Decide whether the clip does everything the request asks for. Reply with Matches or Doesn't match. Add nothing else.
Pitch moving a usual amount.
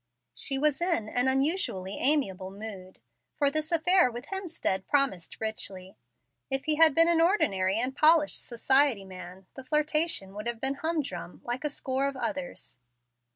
Doesn't match